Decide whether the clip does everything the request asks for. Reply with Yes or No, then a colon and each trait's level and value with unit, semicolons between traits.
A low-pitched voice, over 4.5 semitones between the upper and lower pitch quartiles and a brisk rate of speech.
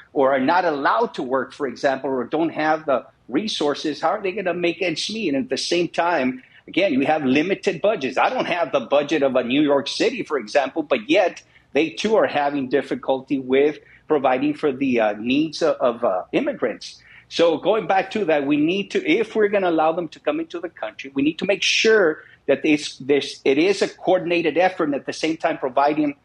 No: medium, 160 Hz; wide, 5.4 semitones; fast, 225 wpm